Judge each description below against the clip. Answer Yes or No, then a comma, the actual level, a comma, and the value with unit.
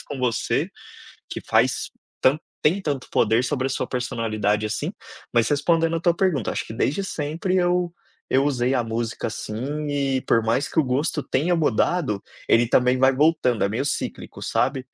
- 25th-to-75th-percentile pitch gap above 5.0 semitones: No, average, 4.6 semitones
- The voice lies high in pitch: No, low, 135 Hz